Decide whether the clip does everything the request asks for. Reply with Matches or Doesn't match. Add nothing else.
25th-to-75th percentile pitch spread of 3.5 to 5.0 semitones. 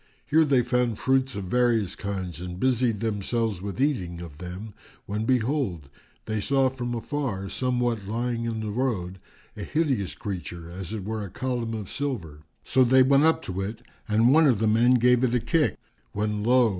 Matches